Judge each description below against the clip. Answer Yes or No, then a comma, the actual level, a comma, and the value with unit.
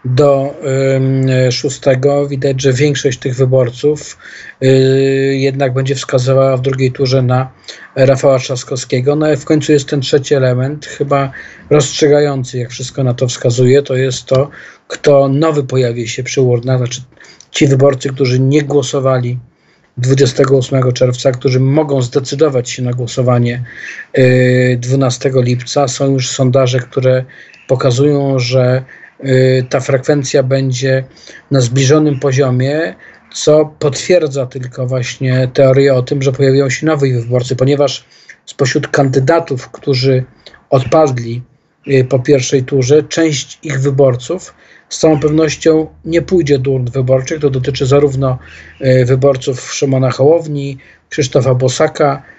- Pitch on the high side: No, low, 135 Hz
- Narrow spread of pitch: Yes, narrow, 1.7 semitones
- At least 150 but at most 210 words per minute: No, average, 125 wpm